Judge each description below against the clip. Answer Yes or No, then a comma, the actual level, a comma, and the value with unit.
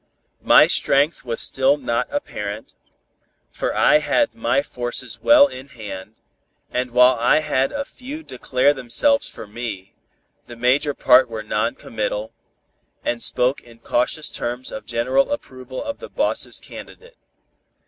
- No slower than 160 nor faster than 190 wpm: No, average, 140 wpm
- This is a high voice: No, low, 125 Hz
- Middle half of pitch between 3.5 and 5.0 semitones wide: Yes, average, 4.0 semitones